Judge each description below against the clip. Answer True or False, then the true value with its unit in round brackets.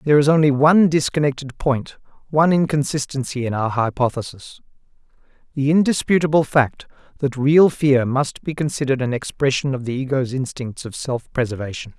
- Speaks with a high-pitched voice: False (135 Hz)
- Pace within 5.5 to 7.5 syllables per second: True (5.6 syllables/s)